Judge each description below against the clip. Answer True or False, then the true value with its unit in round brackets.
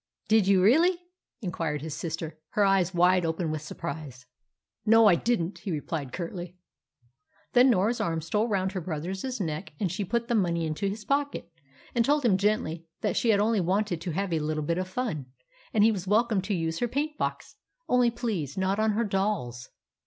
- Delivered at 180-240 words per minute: True (195 wpm)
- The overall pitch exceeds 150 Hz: True (190 Hz)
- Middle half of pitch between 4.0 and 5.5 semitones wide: True (4.9 semitones)